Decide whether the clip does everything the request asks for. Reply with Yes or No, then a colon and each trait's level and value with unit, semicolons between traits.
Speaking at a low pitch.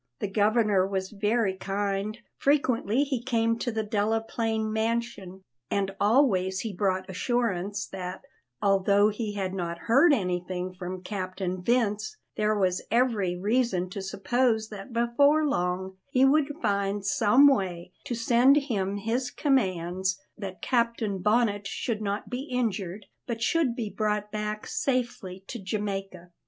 No: high, 210 Hz